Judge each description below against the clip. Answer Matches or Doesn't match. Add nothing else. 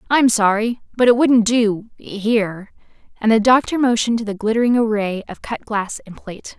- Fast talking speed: Doesn't match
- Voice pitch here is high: Matches